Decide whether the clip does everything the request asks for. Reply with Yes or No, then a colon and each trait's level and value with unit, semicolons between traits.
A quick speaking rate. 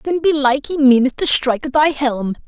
Yes: fast, 220 wpm